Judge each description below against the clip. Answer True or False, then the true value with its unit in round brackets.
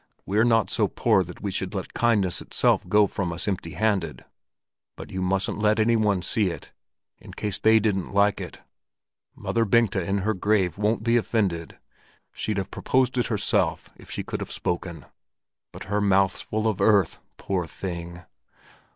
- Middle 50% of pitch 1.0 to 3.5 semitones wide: True (2.9 semitones)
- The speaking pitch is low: True (100 Hz)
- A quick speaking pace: False (175 wpm)